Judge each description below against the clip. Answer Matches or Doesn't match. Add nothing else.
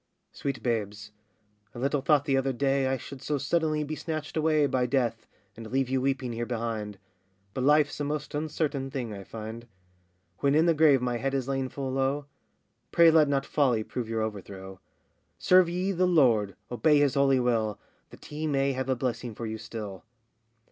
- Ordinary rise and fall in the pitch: Matches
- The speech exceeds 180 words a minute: Matches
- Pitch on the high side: Doesn't match